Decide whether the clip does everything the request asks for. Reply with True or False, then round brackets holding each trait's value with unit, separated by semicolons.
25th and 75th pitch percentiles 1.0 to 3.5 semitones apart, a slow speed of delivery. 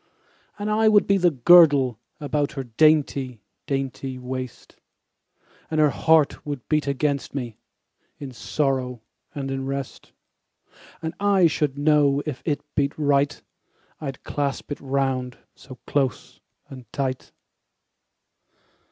True (2.6 semitones; 125 wpm)